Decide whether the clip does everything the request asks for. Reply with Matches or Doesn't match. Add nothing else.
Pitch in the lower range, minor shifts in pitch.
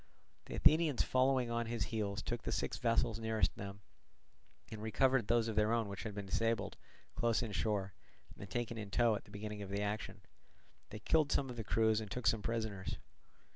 Matches